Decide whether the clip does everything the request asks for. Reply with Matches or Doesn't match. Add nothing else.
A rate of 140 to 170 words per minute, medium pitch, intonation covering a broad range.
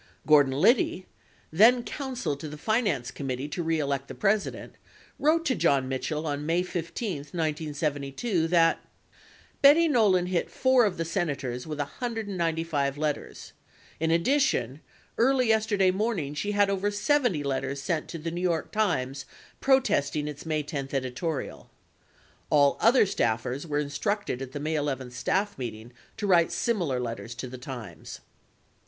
Matches